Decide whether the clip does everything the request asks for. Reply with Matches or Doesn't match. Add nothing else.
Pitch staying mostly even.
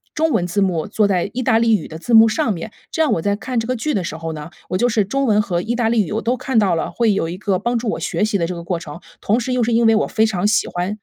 Doesn't match